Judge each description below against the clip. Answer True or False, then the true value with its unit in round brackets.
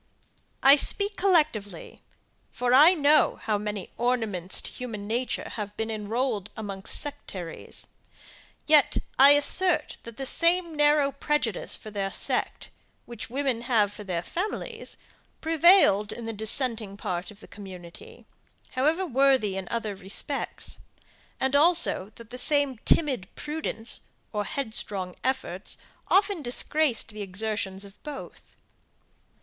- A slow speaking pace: True (130 wpm)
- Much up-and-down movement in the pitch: True (6.1 semitones)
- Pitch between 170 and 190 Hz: False (240 Hz)